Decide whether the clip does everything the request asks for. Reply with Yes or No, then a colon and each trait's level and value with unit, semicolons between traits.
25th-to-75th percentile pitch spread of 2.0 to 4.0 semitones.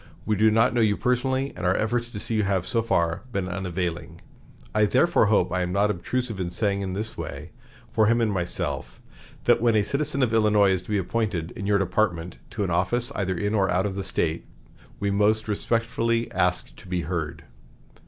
Yes: average, 3.7 semitones